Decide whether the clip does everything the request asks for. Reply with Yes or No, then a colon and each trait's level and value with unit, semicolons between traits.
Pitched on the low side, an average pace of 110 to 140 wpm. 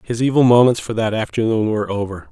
No: low, 110 Hz; fast, 205 wpm